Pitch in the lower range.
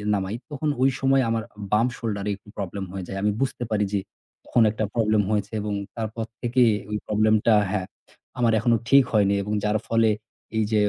Yes: low, 110 Hz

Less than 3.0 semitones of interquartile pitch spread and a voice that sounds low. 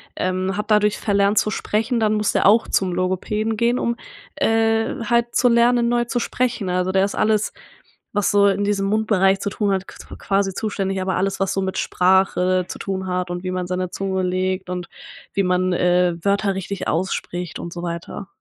No: narrow, 2.5 semitones; high, 195 Hz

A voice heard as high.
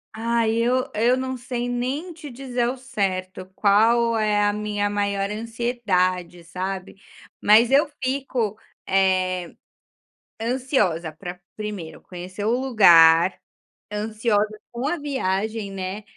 Yes: high, 215 Hz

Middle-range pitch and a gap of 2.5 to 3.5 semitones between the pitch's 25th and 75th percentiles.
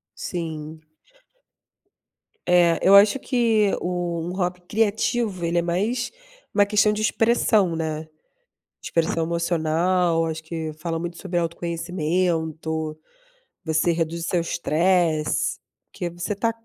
Yes: medium, 170 Hz; average, 2.8 semitones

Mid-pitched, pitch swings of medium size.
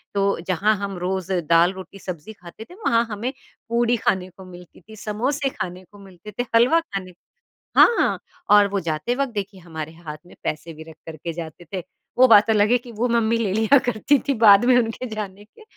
No: high, 200 Hz; average, 4.4 semitones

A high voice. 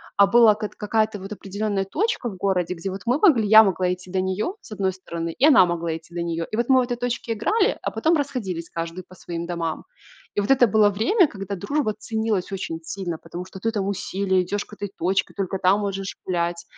Yes: high, 195 Hz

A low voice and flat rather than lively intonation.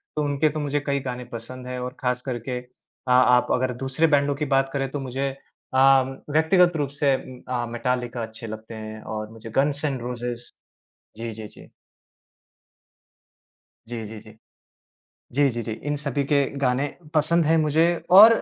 No: low, 130 Hz; average, 3.0 semitones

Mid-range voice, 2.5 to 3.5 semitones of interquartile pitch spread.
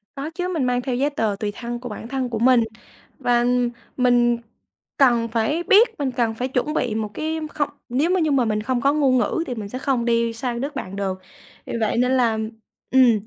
No: high, 245 Hz; average, 2.9 semitones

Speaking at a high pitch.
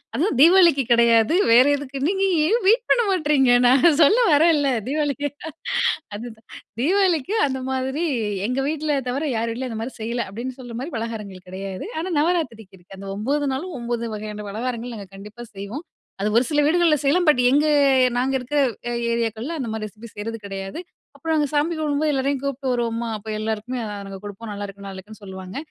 Yes: very high, 255 Hz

